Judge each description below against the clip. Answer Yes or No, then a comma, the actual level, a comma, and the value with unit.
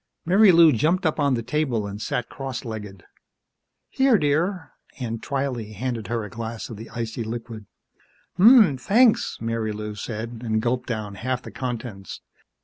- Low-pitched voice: Yes, low, 120 Hz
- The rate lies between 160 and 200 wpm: No, average, 150 wpm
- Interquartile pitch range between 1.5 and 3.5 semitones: No, average, 4.9 semitones